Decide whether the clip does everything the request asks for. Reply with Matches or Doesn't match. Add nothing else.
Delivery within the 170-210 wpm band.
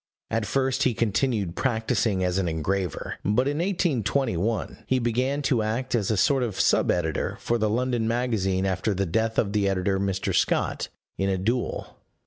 Matches